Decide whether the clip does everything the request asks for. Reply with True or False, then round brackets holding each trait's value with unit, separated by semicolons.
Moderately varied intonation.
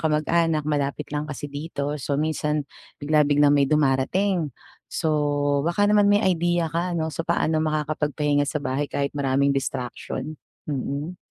False (2.2 semitones)